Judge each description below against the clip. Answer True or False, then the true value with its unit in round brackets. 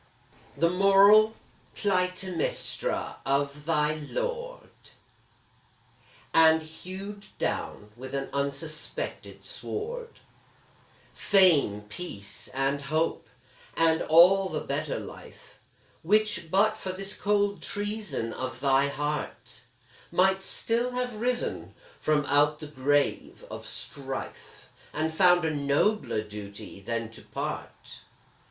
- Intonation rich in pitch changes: True (6.1 semitones)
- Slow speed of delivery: True (105 wpm)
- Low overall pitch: False (160 Hz)